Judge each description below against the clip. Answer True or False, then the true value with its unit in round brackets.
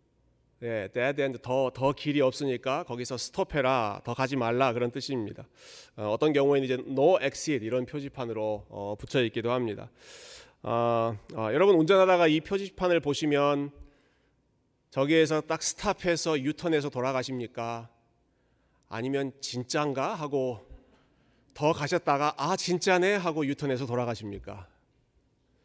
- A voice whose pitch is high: False (135 Hz)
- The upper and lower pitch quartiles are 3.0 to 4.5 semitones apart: True (4.0 semitones)